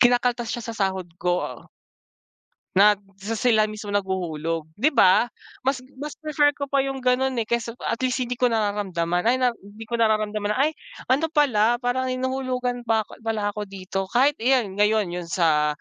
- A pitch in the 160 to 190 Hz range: No, high, 225 Hz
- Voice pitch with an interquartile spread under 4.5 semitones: Yes, average, 4.1 semitones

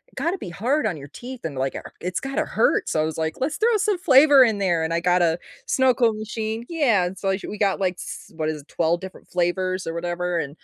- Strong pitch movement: Yes, wide, 7.0 semitones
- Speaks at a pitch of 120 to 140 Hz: No, high, 190 Hz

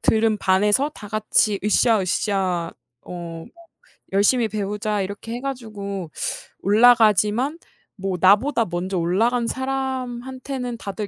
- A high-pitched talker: Yes, high, 210 Hz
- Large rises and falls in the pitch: No, average, 3.9 semitones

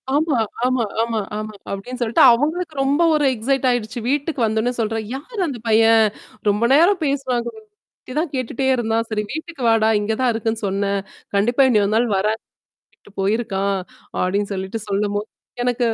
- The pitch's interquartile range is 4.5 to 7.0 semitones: No, average, 3.9 semitones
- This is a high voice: Yes, high, 230 Hz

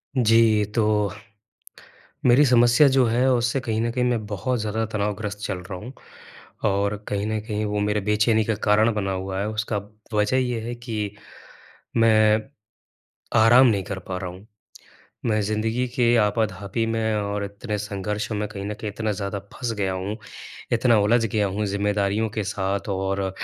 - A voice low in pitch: Yes, low, 105 Hz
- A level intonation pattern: Yes, narrow, 2.0 semitones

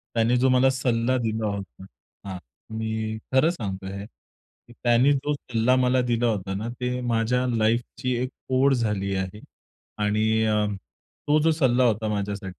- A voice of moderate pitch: No, low, 115 Hz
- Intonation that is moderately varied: Yes, average, 3.1 semitones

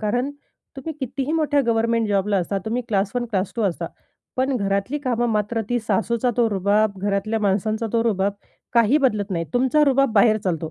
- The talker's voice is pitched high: Yes, high, 225 Hz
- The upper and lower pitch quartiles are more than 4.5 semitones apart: No, average, 3.6 semitones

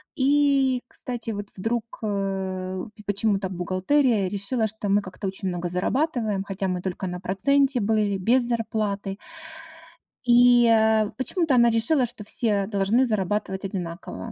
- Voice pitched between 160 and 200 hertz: No, high, 210 Hz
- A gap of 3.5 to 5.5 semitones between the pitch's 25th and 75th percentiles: Yes, average, 3.9 semitones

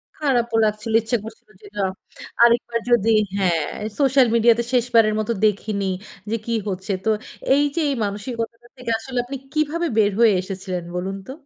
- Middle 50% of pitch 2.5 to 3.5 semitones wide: Yes, average, 2.8 semitones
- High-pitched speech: Yes, high, 230 Hz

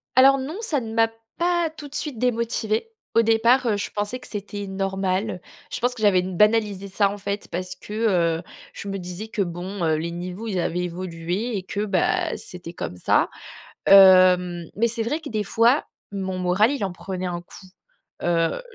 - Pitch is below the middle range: No, high, 200 Hz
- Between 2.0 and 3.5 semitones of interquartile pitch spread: No, average, 3.9 semitones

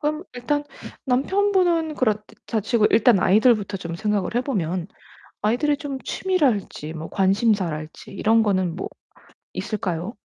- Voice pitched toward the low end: No, high, 215 Hz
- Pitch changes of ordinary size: No, wide, 6.4 semitones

